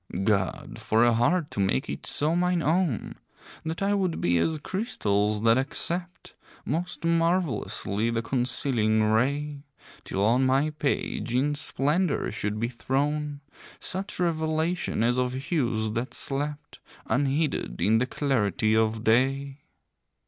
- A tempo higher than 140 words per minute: No, slow, 135 wpm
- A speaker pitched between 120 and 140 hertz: Yes, low, 135 Hz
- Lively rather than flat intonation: Yes, wide, 5.9 semitones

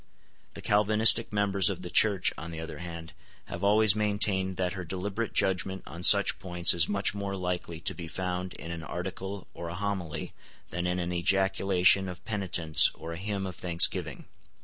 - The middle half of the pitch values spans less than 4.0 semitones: Yes, narrow, 2.5 semitones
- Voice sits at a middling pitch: No, very low, 95 Hz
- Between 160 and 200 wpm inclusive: Yes, average, 180 wpm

